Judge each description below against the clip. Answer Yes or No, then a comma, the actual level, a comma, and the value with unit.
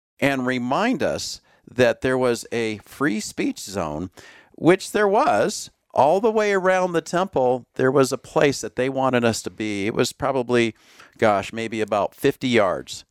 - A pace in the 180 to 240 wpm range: No, average, 170 wpm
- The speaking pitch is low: Yes, low, 130 Hz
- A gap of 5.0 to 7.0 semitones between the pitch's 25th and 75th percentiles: Yes, wide, 5.5 semitones